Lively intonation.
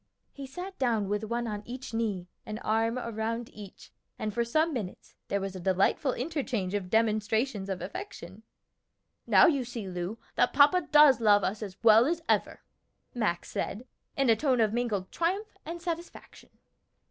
No: average, 4.6 semitones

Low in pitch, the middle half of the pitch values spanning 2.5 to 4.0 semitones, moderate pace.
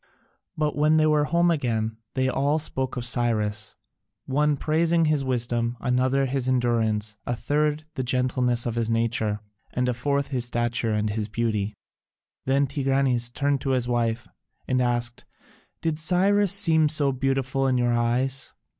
Yes: low, 130 Hz; average, 3.4 semitones; average, 155 wpm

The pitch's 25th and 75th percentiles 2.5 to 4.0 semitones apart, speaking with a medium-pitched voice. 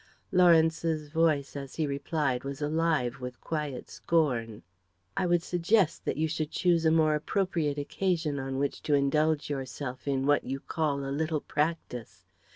Yes: average, 2.9 semitones; medium, 150 Hz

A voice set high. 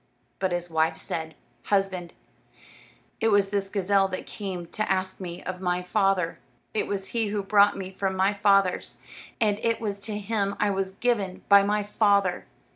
Yes: high, 195 Hz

